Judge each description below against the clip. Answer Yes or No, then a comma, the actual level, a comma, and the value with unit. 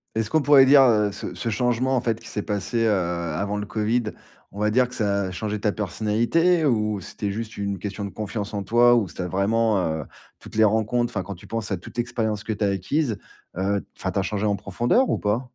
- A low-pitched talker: Yes, low, 105 Hz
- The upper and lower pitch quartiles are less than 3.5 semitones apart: Yes, average, 2.8 semitones